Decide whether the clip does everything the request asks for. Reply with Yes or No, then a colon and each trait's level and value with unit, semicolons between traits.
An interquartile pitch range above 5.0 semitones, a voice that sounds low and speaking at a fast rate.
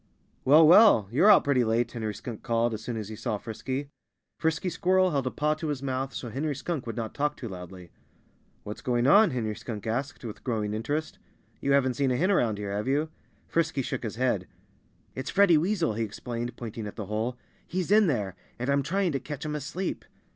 Yes: wide, 5.4 semitones; low, 130 Hz; fast, 215 wpm